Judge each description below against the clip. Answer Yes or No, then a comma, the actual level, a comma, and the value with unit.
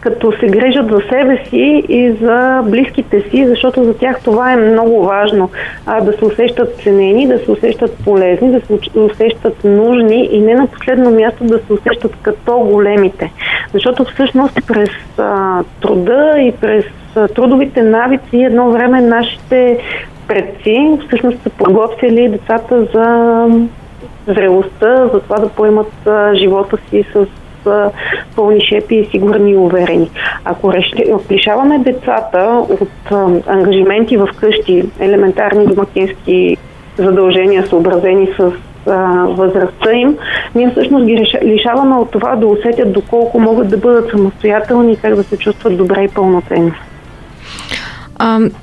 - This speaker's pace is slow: No, average, 135 wpm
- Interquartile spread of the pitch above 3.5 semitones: No, average, 3.2 semitones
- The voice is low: No, high, 220 Hz